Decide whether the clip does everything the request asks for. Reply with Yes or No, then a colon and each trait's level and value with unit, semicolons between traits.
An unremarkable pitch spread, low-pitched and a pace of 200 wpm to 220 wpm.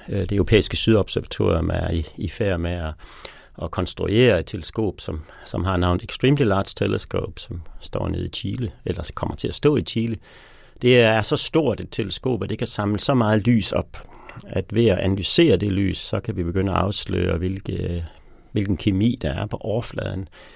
No: average, 3.9 semitones; low, 100 Hz; average, 190 wpm